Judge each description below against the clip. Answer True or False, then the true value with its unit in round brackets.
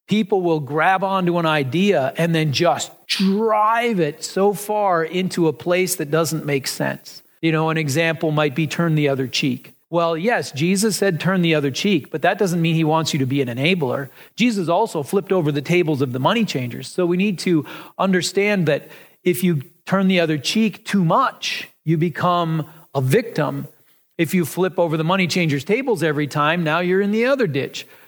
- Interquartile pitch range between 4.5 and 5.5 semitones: False (3.8 semitones)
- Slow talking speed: False (200 wpm)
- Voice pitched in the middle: True (170 Hz)